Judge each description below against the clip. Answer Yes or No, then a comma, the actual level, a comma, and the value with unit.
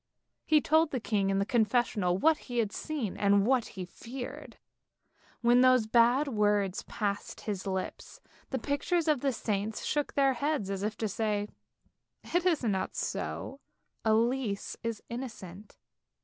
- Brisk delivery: No, average, 150 wpm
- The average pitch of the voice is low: No, high, 230 Hz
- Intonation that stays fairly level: No, average, 4.8 semitones